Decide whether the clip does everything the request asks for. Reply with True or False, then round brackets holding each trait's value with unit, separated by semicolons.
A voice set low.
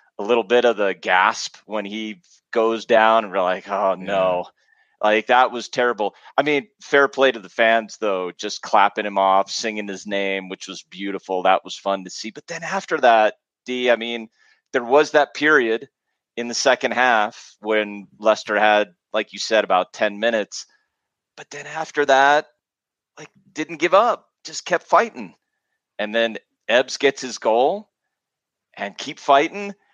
True (115 Hz)